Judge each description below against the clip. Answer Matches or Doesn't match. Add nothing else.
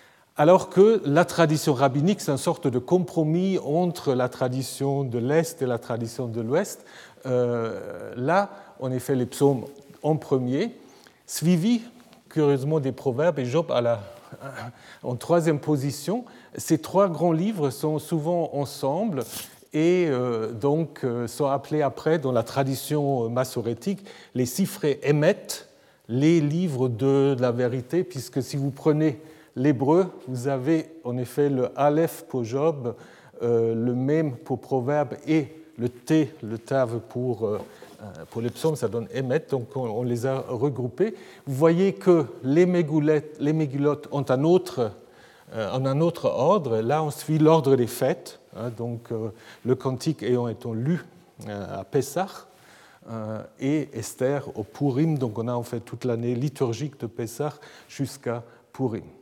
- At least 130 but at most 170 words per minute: Matches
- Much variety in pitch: Doesn't match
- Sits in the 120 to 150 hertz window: Matches